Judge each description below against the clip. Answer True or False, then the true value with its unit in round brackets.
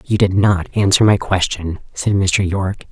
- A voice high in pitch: False (95 Hz)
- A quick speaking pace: False (185 wpm)